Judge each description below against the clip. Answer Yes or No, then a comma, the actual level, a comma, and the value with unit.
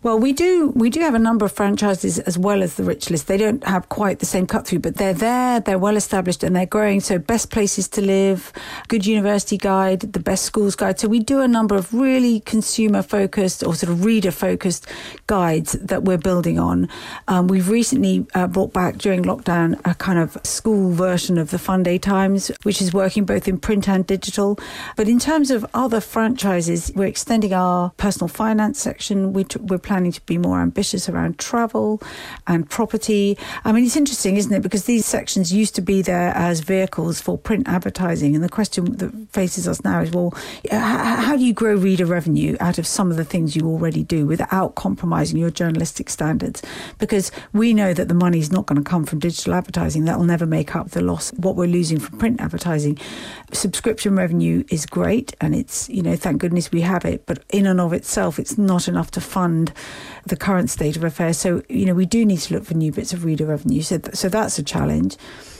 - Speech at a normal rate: No, fast, 215 wpm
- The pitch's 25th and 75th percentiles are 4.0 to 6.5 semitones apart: No, average, 3.5 semitones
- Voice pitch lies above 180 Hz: Yes, high, 190 Hz